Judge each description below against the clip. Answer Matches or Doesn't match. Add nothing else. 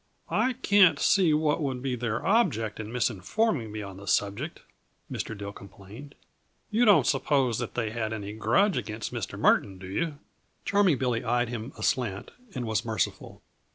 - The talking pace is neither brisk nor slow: Matches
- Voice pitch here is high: Doesn't match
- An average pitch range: Doesn't match